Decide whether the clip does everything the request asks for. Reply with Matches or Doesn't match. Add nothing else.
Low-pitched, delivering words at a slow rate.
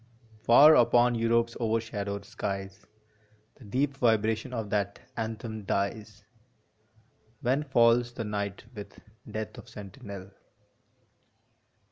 Matches